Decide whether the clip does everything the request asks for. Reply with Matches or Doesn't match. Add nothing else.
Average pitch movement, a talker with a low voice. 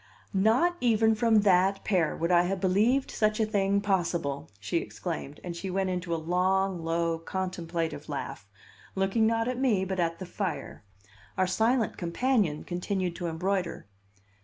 Doesn't match